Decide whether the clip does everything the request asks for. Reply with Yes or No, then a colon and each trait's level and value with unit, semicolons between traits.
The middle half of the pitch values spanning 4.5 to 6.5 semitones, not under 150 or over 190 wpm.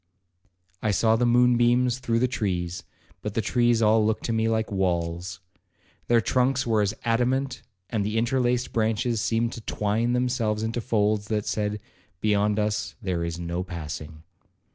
No: average, 2.7 semitones; average, 165 wpm